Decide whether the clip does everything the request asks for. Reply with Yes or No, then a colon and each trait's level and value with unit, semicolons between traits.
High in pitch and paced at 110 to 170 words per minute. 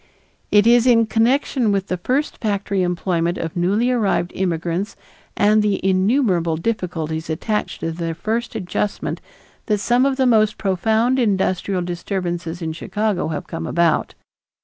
Yes: high, 195 Hz; average, 145 wpm